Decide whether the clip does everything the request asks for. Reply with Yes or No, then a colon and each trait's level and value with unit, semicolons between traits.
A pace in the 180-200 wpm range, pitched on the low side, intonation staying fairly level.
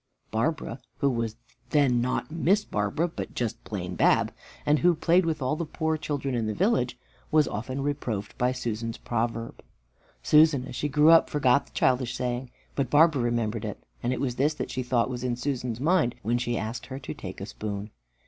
No: average, 195 wpm; low, 125 Hz; average, 4.3 semitones